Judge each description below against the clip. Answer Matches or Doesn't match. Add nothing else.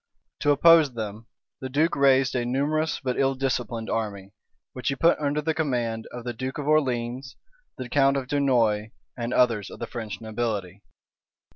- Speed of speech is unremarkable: Matches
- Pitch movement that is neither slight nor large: Matches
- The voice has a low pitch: Matches